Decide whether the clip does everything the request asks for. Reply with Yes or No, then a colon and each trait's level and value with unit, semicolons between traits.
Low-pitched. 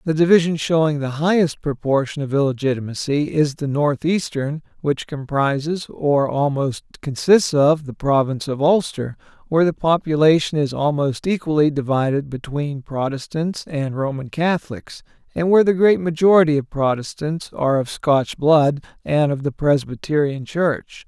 No: medium, 145 Hz